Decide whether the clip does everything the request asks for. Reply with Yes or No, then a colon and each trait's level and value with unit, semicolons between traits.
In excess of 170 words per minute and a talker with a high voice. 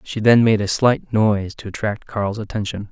No: fast, 205 wpm; low, 110 Hz